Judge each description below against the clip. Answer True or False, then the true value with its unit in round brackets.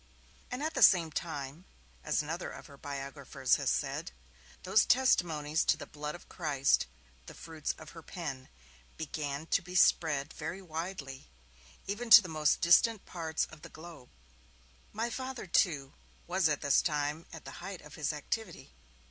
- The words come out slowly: False (160 wpm)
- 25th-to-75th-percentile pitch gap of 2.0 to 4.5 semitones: True (4.0 semitones)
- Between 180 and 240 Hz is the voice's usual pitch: False (160 Hz)